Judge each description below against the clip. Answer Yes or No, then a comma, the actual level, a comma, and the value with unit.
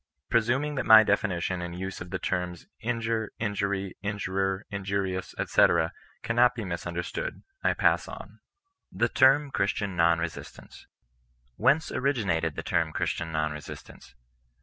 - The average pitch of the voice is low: Yes, low, 100 Hz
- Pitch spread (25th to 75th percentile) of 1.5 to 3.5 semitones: No, average, 4.7 semitones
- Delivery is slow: Yes, slow, 130 wpm